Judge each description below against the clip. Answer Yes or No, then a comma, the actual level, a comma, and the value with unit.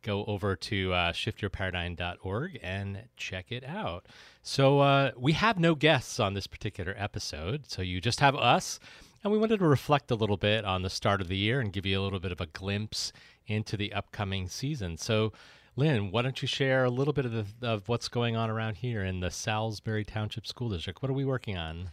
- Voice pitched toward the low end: Yes, low, 110 Hz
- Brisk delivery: Yes, fast, 215 wpm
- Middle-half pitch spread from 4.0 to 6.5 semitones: Yes, average, 4.9 semitones